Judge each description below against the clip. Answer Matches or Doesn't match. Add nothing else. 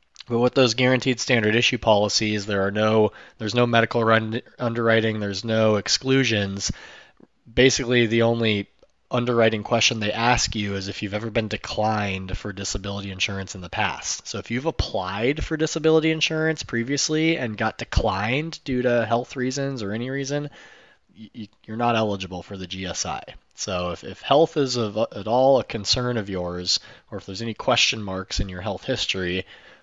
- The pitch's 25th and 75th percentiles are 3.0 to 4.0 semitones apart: Matches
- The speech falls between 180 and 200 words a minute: Doesn't match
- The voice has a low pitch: Matches